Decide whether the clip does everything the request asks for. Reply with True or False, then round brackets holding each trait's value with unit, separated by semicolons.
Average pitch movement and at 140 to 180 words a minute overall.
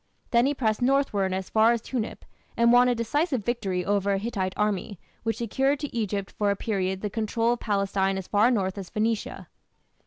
False (3.2 semitones; 195 wpm)